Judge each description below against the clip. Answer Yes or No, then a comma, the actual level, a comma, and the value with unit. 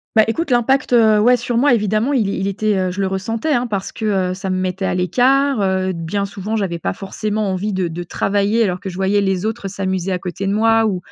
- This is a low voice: No, high, 200 Hz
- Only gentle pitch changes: No, average, 3.0 semitones